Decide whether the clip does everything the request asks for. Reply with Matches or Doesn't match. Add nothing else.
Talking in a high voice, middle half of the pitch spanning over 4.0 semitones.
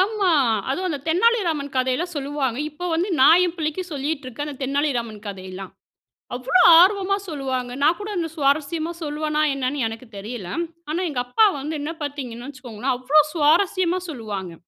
Matches